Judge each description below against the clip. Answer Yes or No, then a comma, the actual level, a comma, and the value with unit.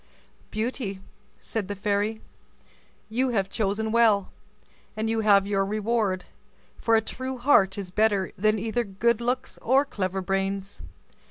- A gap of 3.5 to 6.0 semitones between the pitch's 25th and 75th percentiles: No, average, 2.8 semitones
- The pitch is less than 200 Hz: No, high, 215 Hz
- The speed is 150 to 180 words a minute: No, average, 140 wpm